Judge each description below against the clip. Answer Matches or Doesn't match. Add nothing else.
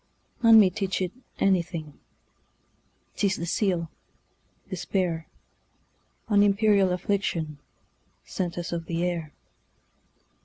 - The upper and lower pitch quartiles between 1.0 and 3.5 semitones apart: Matches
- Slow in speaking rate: Matches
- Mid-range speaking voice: Matches